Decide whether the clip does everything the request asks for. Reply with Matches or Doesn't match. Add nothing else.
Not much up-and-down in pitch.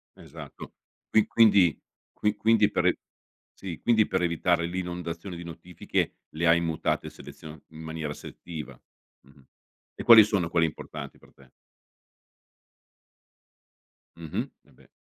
Doesn't match